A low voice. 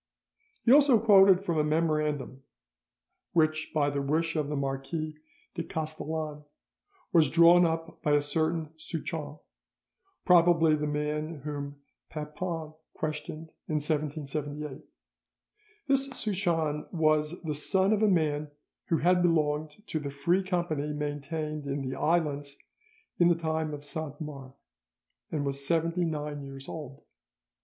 No: medium, 155 Hz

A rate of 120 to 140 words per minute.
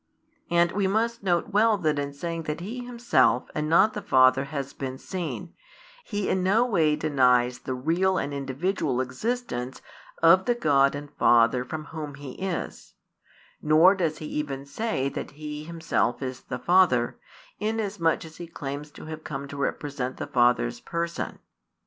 No: average, 165 wpm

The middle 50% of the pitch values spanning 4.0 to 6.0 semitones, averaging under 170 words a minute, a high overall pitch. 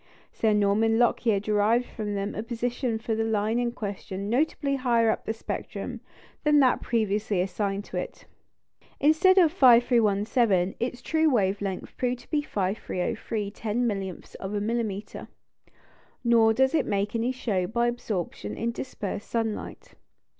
No: average, 3.1 semitones; average, 155 wpm; high, 225 Hz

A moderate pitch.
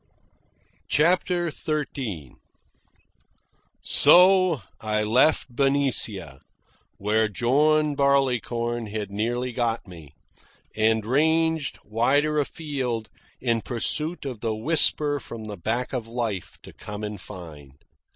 No: low, 120 Hz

